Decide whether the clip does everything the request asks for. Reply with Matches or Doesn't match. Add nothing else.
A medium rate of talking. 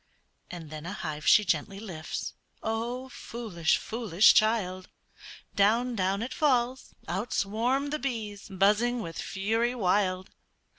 Doesn't match